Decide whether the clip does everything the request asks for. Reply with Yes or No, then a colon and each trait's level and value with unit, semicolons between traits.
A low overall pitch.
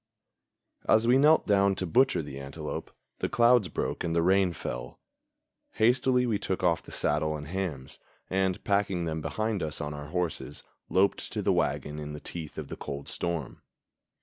Yes: very low, 90 Hz